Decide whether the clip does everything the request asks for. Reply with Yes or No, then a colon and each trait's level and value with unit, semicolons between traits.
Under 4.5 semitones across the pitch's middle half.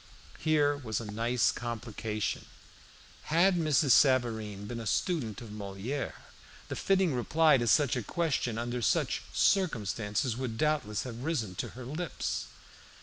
No: wide, 5.5 semitones